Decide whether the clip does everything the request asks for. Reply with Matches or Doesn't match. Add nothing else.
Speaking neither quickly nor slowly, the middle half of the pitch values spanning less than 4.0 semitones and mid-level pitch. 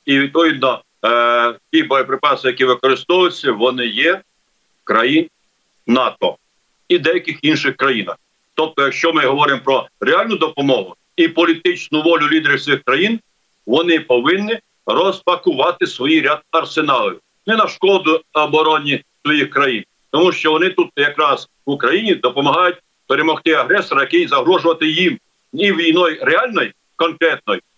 Doesn't match